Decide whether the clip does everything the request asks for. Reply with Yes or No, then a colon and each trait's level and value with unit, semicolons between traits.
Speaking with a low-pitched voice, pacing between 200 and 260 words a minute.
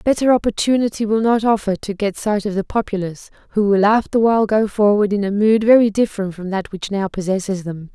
No: high, 210 Hz; fast, 205 wpm